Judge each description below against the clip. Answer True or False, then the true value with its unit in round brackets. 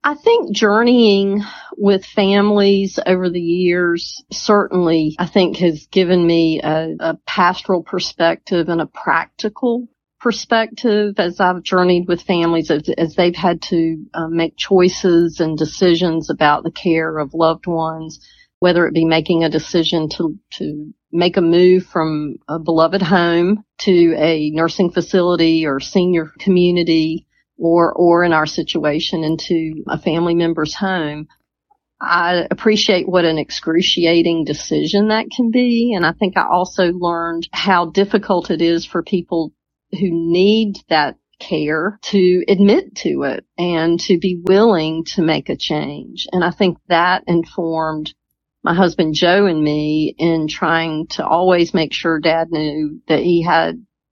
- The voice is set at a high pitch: False (175 Hz)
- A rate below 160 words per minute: True (145 wpm)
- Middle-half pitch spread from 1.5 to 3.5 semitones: True (2.4 semitones)